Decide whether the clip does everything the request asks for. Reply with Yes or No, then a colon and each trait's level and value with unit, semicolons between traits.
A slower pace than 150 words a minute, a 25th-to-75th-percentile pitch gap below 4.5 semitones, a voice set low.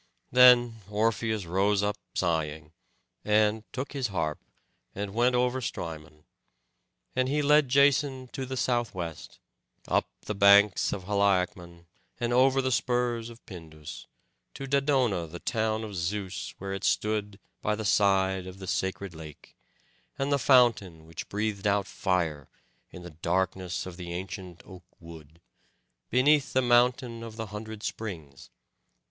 No: average, 140 wpm; average, 5.2 semitones; low, 105 Hz